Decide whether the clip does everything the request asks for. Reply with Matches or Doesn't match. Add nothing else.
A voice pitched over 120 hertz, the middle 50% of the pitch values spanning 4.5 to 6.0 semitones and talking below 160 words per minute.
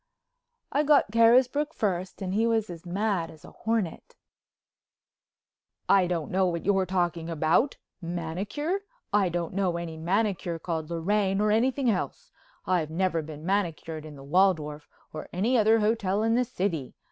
Matches